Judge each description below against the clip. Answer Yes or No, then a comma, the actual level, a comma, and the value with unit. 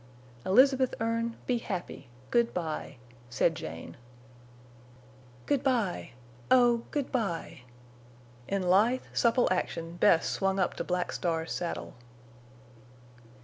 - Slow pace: Yes, slow, 100 wpm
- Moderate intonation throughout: No, wide, 6.3 semitones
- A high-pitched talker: Yes, high, 195 Hz